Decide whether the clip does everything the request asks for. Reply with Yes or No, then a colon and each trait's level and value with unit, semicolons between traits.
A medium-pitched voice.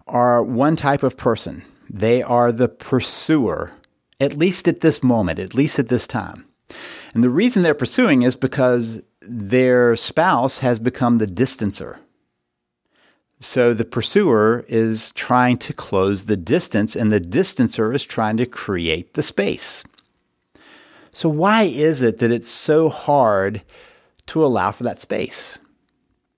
No: low, 120 Hz